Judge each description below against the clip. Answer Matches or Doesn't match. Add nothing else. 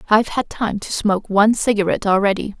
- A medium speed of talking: Matches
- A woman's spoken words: Matches